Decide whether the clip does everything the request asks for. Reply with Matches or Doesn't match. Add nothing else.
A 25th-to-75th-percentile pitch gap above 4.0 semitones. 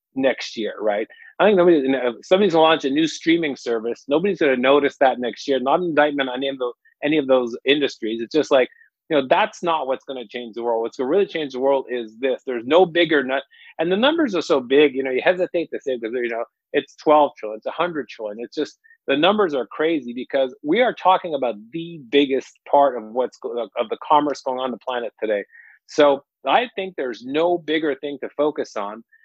Matches